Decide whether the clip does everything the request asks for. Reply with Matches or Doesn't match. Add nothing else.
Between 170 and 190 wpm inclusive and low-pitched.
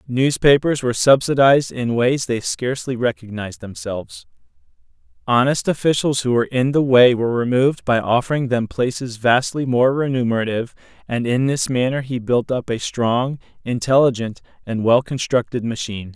Doesn't match